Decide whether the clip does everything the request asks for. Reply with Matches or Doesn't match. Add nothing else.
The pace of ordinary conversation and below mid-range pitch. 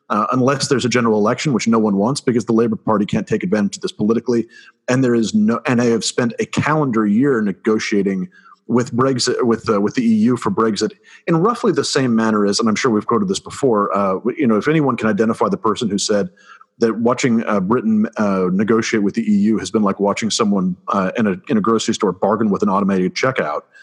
Doesn't match